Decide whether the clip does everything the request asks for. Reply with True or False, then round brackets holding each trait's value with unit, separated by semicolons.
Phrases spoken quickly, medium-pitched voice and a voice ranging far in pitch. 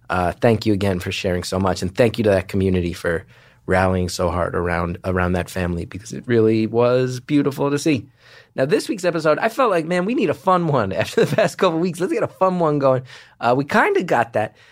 False (245 wpm; 120 Hz; 8.6 semitones)